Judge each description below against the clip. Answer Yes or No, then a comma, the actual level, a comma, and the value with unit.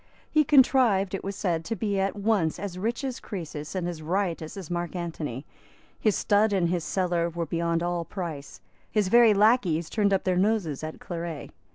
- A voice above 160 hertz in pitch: Yes, medium, 185 Hz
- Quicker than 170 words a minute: Yes, average, 190 wpm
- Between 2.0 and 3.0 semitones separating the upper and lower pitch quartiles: No, average, 3.6 semitones